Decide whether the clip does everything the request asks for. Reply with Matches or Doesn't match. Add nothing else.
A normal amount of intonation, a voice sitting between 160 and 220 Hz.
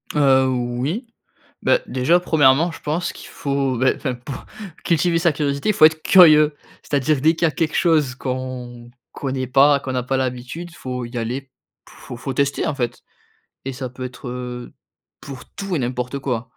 Doesn't match